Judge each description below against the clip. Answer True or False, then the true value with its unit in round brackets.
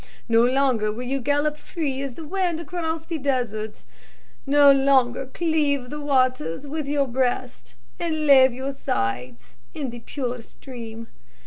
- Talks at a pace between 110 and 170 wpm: True (145 wpm)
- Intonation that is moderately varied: True (3.3 semitones)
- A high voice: True (270 Hz)